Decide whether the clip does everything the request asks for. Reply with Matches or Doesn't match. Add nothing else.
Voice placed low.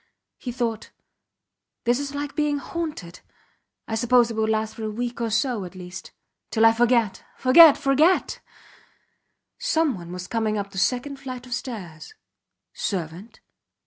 Doesn't match